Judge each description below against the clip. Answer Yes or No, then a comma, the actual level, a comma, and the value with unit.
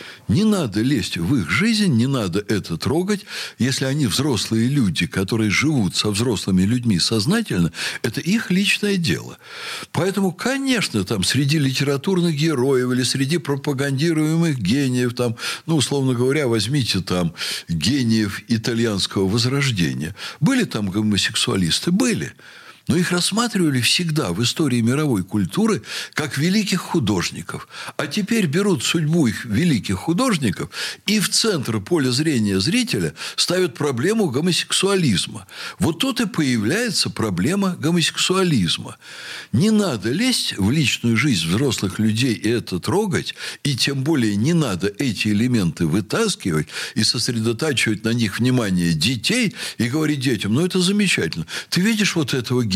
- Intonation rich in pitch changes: Yes, wide, 8.0 semitones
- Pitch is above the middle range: No, medium, 140 Hz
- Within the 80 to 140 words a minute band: Yes, average, 130 wpm